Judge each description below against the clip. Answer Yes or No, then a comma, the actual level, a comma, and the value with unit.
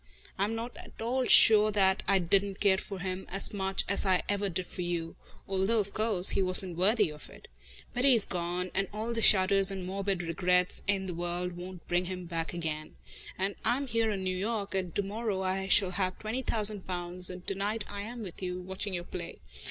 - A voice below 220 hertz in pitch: Yes, high, 190 Hz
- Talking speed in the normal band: No, fast, 220 wpm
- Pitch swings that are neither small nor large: No, narrow, 2.2 semitones